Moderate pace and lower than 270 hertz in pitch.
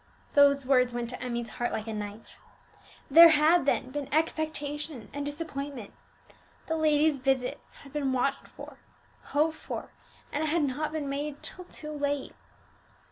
No: average, 155 wpm; very high, 285 Hz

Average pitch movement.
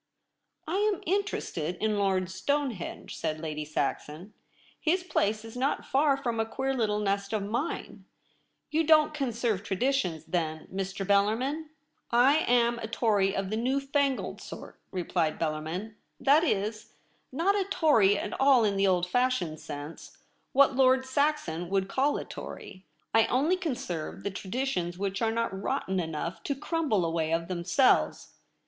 No: wide, 6.7 semitones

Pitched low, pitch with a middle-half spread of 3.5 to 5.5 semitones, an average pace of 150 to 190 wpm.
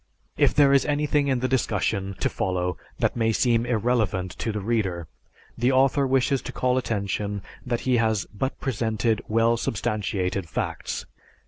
Yes: low, 115 Hz; average, 4.2 semitones; average, 155 wpm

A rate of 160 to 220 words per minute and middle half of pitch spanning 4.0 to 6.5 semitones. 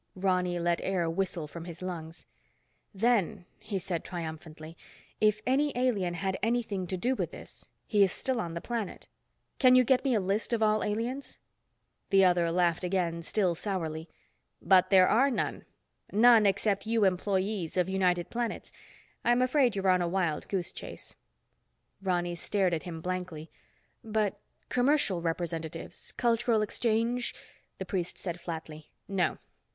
No: average, 150 wpm; average, 4.3 semitones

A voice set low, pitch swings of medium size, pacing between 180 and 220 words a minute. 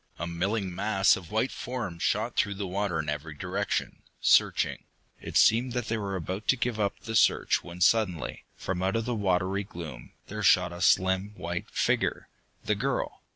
Yes: very low, 95 Hz; average, 3.7 semitones; average, 185 wpm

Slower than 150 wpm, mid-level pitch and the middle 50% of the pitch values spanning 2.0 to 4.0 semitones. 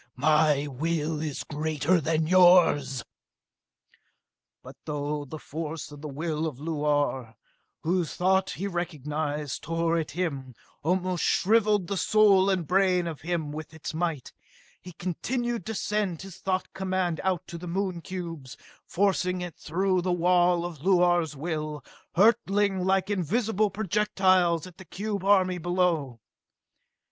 Yes: average, 140 wpm; medium, 175 Hz; average, 3.5 semitones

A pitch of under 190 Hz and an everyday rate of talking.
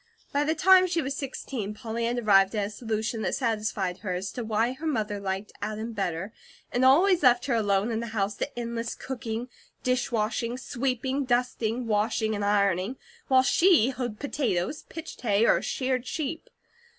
No: high, 230 Hz; average, 175 wpm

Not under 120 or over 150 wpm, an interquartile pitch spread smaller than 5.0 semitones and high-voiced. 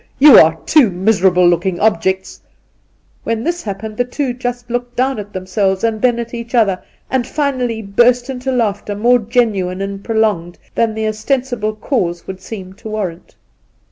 No: average, 175 wpm; average, 4.1 semitones; high, 220 Hz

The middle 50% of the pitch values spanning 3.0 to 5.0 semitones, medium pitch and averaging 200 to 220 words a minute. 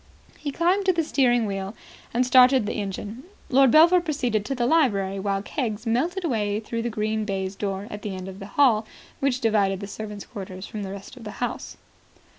No: average, 4.7 semitones; high, 220 Hz; fast, 205 wpm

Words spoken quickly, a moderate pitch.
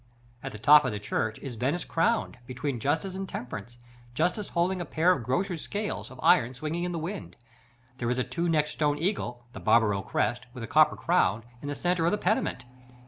Yes: fast, 210 wpm; medium, 145 Hz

